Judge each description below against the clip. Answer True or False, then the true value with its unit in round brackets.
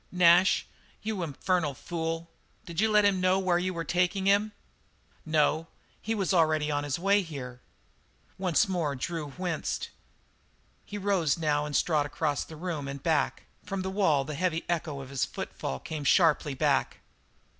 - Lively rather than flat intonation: False (3.9 semitones)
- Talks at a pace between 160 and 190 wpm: True (165 wpm)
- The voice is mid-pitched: True (165 Hz)